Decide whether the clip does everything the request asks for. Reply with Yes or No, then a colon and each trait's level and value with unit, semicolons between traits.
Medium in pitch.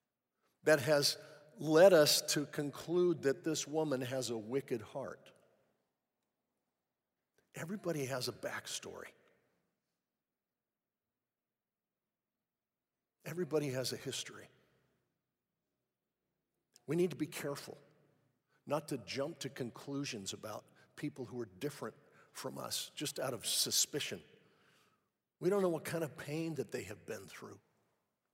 Yes: medium, 145 Hz